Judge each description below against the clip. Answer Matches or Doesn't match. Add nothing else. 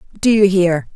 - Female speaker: Matches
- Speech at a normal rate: Matches